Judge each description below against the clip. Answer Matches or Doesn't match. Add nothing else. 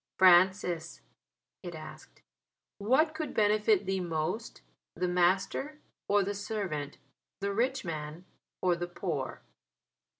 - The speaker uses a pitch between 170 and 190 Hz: Matches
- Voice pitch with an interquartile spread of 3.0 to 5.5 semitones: Matches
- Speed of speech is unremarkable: Doesn't match